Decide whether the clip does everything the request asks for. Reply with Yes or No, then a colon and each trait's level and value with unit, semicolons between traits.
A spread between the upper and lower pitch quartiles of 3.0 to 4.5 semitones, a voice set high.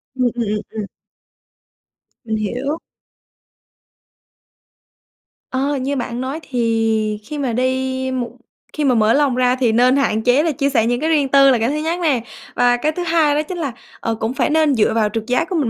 Yes: average, 3.8 semitones; very high, 255 Hz